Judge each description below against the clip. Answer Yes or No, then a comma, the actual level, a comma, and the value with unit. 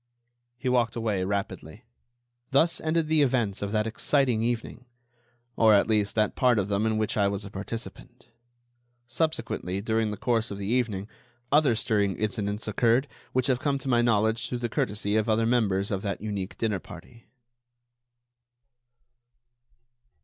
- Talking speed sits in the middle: Yes, average, 155 wpm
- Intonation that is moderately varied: Yes, average, 3.1 semitones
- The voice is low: Yes, low, 110 Hz